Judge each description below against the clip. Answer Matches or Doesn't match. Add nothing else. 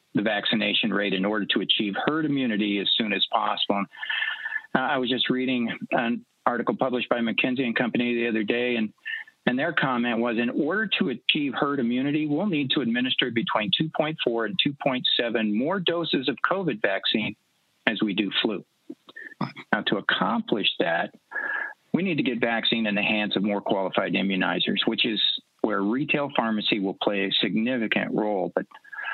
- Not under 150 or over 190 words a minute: Matches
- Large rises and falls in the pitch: Matches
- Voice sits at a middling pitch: Doesn't match